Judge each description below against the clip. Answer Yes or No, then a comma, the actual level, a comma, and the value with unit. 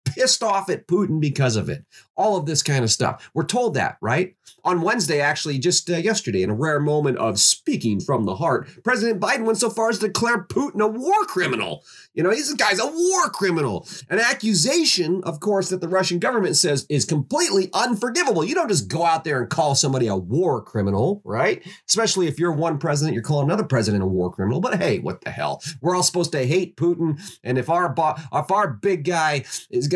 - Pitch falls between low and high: Yes, medium, 170 Hz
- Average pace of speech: No, fast, 215 wpm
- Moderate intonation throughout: No, wide, 6.5 semitones